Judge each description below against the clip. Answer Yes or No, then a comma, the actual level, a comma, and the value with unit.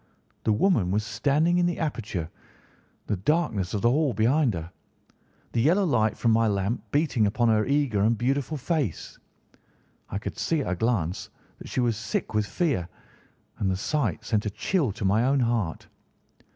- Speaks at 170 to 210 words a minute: Yes, average, 180 wpm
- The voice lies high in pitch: No, low, 115 Hz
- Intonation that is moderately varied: No, wide, 5.9 semitones